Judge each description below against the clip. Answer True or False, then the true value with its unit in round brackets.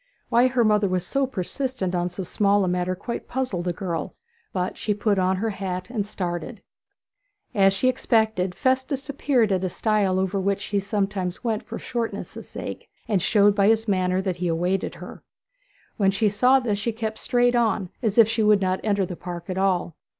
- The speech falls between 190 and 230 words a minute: True (200 wpm)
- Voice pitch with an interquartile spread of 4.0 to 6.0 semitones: False (3.4 semitones)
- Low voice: False (200 Hz)